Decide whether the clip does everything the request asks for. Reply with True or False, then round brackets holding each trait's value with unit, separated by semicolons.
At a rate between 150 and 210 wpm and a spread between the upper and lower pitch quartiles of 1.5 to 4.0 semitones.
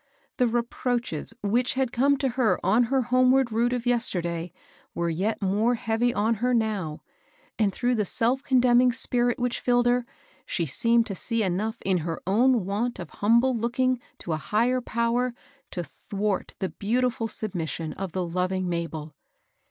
False (165 wpm; 4.4 semitones)